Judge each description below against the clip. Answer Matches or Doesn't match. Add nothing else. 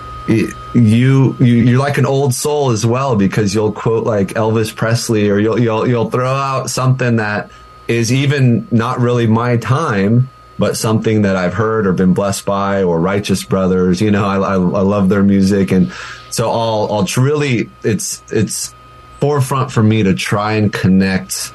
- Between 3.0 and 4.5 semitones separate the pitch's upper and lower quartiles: Matches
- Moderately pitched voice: Doesn't match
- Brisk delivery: Doesn't match